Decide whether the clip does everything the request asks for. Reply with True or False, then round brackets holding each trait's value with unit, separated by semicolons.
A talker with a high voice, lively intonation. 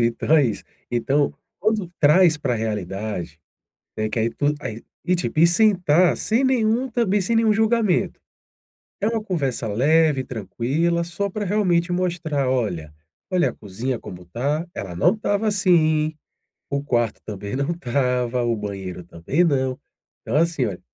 False (150 Hz; 7.8 semitones)